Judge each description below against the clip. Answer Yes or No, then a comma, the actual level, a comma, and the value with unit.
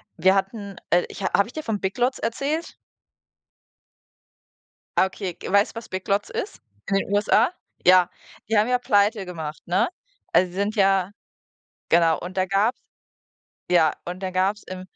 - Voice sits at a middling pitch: No, high, 195 Hz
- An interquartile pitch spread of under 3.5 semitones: Yes, narrow, 2.5 semitones